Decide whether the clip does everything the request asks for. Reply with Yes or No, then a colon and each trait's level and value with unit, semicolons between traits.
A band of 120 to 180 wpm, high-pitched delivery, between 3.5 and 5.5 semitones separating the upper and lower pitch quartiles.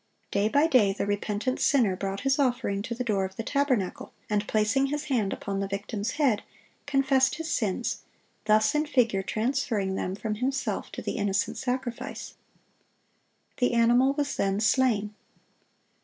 Yes: average, 155 wpm; high, 225 Hz; average, 4.7 semitones